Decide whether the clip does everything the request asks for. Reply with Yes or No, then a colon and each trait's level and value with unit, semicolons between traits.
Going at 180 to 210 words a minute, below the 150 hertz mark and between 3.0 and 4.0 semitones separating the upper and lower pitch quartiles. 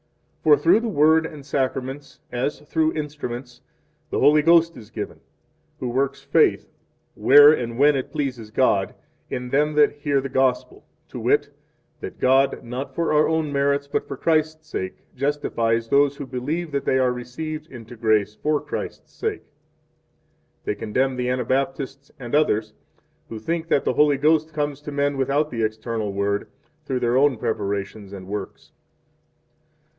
No: average, 165 wpm; low, 135 Hz; average, 3.5 semitones